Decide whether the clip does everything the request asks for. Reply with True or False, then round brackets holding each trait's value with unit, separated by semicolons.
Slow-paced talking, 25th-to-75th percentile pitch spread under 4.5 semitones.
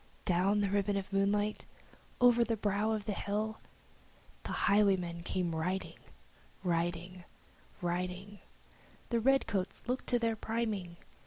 True (125 wpm; 3.1 semitones)